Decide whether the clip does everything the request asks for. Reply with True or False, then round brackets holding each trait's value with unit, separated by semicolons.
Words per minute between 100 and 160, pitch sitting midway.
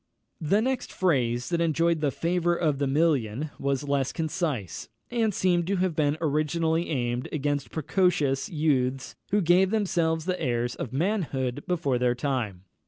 True (155 wpm; 155 Hz)